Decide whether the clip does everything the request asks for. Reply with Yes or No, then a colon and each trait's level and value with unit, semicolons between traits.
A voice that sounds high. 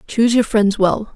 Yes: high, 215 Hz